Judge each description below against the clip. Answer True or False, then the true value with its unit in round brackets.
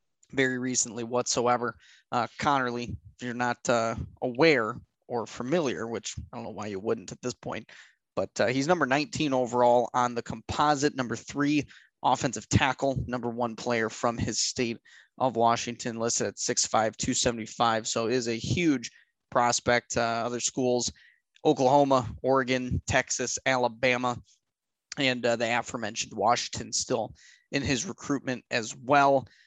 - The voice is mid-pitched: False (120 Hz)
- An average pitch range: False (1.7 semitones)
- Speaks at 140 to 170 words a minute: True (145 wpm)